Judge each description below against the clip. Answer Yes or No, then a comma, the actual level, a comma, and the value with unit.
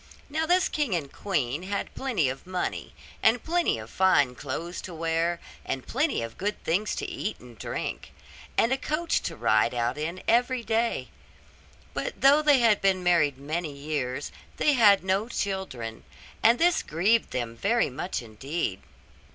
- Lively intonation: Yes, wide, 8.6 semitones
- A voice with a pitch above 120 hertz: Yes, medium, 185 Hz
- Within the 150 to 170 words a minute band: Yes, average, 165 wpm